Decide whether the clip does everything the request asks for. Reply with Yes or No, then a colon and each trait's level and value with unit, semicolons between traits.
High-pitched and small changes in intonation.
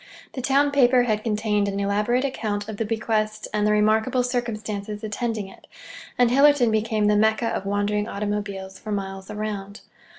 Yes: high, 215 Hz; narrow, 2.3 semitones